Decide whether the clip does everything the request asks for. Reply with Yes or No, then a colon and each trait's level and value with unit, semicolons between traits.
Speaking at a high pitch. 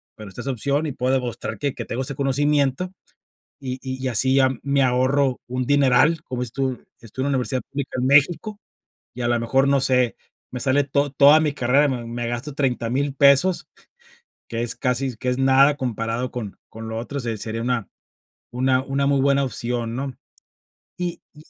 No: low, 130 Hz